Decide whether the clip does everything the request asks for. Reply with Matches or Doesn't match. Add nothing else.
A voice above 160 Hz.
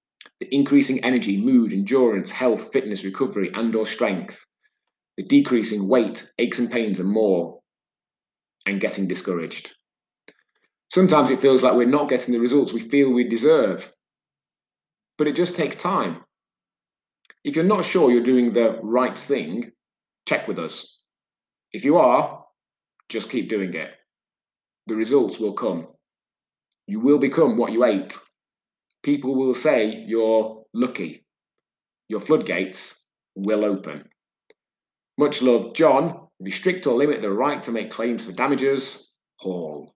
Doesn't match